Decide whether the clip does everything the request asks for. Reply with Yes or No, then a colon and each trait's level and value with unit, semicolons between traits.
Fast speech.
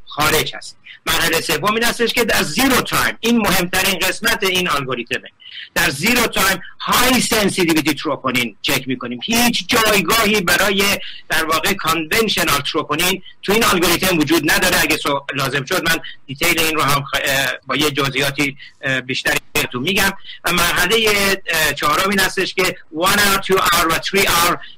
No: average, 145 wpm